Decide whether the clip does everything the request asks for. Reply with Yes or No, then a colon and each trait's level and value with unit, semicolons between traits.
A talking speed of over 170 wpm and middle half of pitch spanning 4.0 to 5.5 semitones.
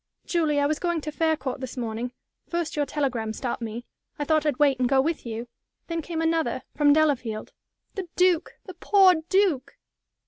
Yes: average, 180 wpm; average, 4.5 semitones